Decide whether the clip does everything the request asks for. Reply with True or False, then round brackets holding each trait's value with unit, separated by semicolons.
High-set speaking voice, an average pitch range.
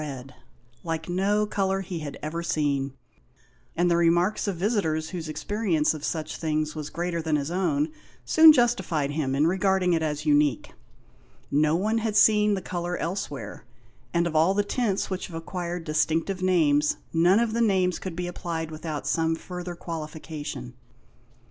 False (170 Hz; 3.6 semitones)